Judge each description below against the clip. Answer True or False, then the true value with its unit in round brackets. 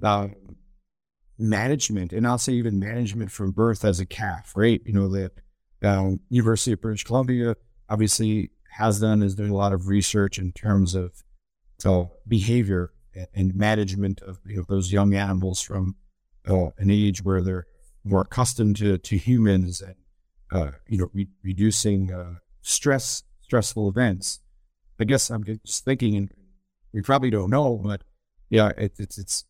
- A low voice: True (100 Hz)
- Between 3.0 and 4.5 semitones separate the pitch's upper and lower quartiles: False (2.5 semitones)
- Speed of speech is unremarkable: True (165 wpm)